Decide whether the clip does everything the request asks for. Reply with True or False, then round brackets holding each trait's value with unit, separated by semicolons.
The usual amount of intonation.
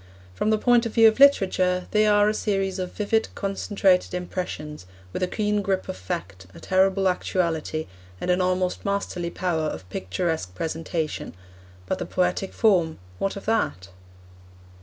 True (3.8 semitones)